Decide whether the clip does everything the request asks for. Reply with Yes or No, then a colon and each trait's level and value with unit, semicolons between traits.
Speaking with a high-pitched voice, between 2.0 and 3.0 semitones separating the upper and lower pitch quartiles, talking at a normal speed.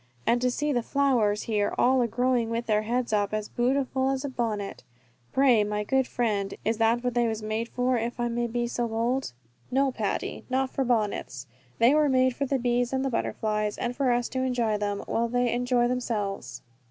No: high, 240 Hz; average, 2.7 semitones; fast, 210 wpm